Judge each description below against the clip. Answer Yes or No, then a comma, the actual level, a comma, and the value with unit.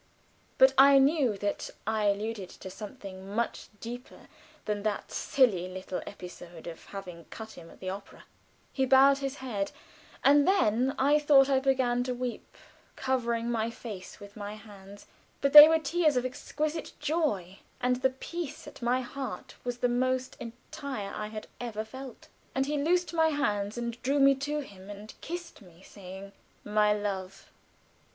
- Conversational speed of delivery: Yes, average, 165 wpm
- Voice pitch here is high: Yes, high, 240 Hz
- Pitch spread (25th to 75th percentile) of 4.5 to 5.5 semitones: Yes, average, 5.0 semitones